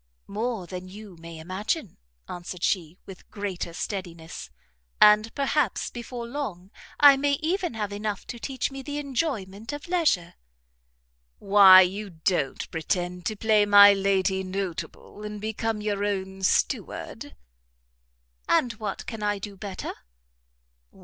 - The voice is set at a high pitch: Yes, high, 205 Hz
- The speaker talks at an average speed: No, slow, 130 wpm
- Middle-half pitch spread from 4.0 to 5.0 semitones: No, average, 3.5 semitones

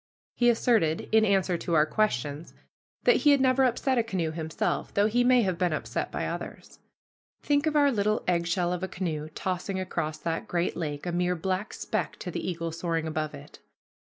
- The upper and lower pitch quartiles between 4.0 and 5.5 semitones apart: Yes, average, 5.2 semitones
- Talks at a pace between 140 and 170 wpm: No, average, 195 wpm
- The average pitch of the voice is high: No, medium, 180 Hz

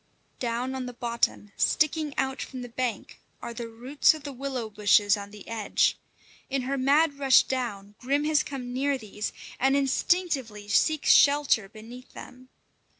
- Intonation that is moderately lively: Yes, average, 3.6 semitones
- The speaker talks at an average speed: Yes, average, 160 wpm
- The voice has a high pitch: Yes, very high, 255 Hz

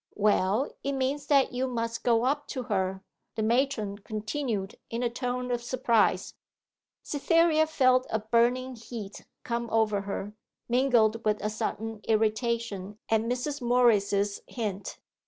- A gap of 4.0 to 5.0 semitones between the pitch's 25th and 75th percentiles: No, average, 3.1 semitones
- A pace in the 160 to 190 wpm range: No, slow, 135 wpm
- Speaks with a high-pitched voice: Yes, high, 235 Hz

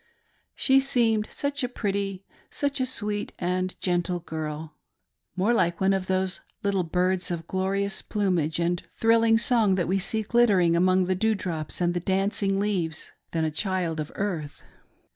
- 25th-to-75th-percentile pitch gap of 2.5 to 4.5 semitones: Yes, average, 3.2 semitones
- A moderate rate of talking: Yes, average, 165 wpm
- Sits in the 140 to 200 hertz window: Yes, high, 190 Hz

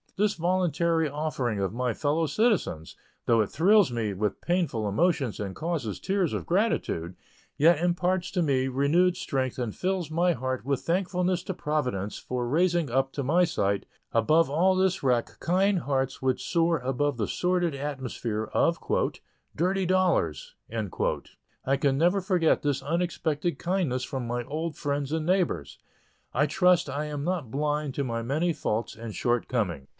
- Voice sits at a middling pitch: Yes, medium, 150 Hz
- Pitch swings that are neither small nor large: No, wide, 5.8 semitones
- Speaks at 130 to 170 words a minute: Yes, average, 160 wpm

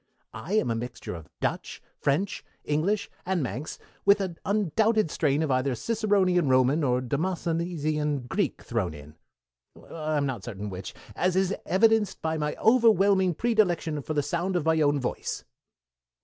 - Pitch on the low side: No, medium, 160 Hz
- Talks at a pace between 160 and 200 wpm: No, average, 150 wpm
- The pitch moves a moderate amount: No, wide, 5.8 semitones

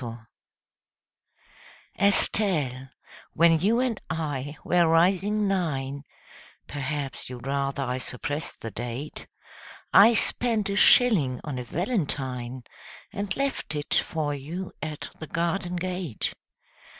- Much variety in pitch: Yes, wide, 5.9 semitones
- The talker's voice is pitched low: No, medium, 160 Hz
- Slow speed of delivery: Yes, slow, 115 wpm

